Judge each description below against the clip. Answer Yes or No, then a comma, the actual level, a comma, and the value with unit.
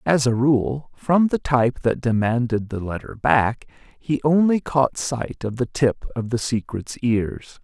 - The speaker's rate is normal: Yes, average, 175 wpm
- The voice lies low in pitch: Yes, low, 125 Hz